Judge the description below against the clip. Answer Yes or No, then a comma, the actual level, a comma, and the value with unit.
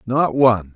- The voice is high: No, low, 120 Hz